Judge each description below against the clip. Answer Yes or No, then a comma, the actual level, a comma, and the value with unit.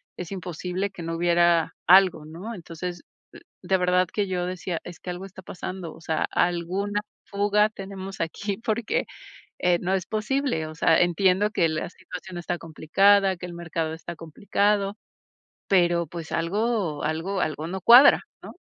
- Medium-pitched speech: Yes, medium, 180 Hz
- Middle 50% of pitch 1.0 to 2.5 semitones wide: No, average, 2.9 semitones